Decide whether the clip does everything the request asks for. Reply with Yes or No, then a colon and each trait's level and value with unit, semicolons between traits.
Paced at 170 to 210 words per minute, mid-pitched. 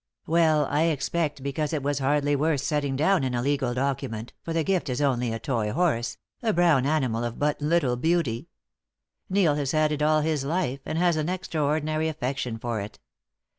Yes: average, 190 wpm; medium, 145 Hz